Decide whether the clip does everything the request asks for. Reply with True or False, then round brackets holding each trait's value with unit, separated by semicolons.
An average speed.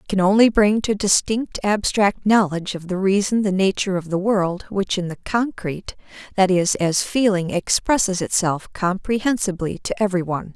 True (170 wpm)